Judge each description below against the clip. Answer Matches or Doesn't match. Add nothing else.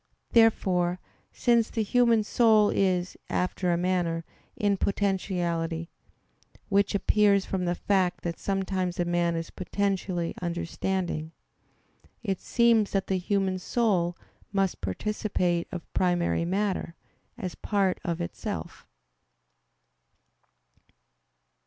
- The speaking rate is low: Matches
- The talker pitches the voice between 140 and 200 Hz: Matches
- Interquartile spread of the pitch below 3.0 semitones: Matches